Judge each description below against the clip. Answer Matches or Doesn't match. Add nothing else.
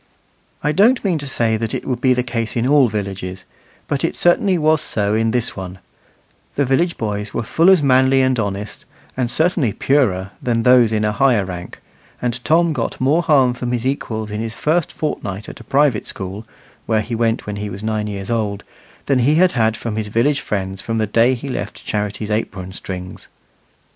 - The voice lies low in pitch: Matches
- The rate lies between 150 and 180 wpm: Doesn't match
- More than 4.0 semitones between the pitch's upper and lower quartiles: Matches